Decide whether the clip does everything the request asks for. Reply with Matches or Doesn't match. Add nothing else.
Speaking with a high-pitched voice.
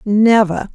Matches